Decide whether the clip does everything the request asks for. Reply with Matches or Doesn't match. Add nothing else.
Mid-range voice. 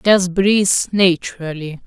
Matches